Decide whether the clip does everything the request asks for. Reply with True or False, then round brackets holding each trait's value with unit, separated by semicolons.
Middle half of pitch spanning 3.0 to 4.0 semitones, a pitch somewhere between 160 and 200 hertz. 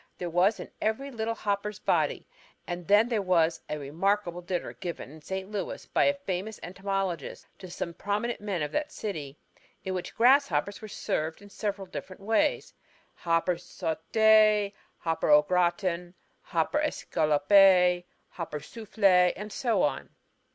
True (3.6 semitones; 190 Hz)